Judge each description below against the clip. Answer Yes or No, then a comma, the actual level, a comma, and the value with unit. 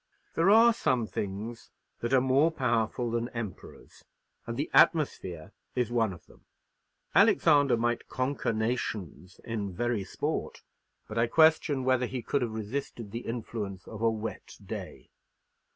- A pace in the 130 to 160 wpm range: Yes, average, 145 wpm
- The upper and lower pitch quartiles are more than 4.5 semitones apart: No, average, 3.1 semitones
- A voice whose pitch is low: Yes, low, 120 Hz